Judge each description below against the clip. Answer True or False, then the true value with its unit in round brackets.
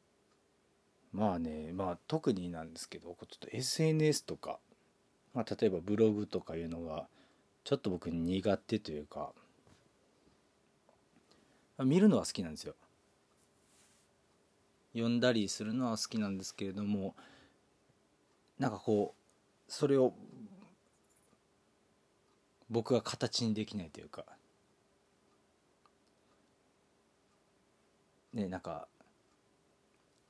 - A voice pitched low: True (105 Hz)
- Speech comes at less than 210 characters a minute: True (200 characters per minute)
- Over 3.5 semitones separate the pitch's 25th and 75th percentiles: True (5.5 semitones)